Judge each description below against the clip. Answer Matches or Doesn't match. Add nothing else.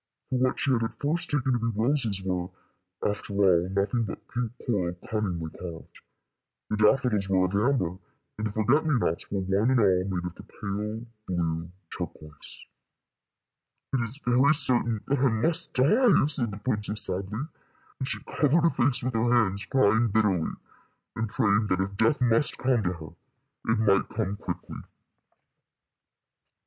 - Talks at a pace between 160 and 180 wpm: Matches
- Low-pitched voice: Matches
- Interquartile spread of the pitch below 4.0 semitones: Doesn't match